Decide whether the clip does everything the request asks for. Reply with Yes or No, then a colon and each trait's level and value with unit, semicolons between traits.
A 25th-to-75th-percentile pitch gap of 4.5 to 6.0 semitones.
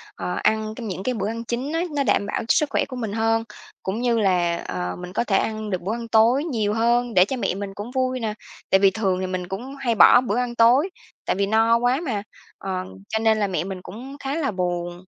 No: average, 4.1 semitones